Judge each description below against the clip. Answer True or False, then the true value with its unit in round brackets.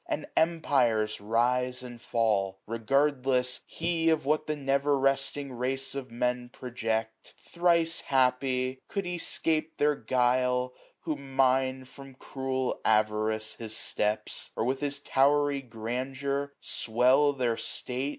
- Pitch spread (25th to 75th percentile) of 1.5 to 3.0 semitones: True (2.6 semitones)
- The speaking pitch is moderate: False (130 Hz)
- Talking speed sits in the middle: False (130 wpm)